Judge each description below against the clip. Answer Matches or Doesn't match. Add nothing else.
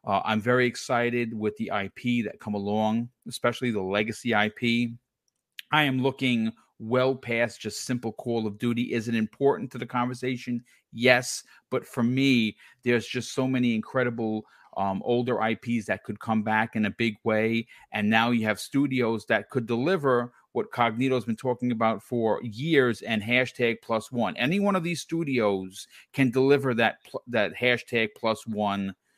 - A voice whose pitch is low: Matches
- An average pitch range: Doesn't match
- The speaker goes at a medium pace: Matches